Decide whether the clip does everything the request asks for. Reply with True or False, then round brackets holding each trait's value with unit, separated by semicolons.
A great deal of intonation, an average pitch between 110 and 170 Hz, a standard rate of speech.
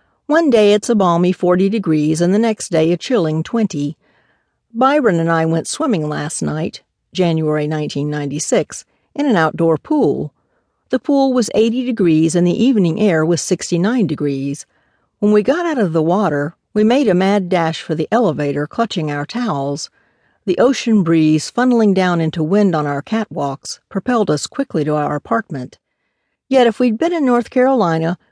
False (6.8 semitones; 180 Hz; 175 wpm)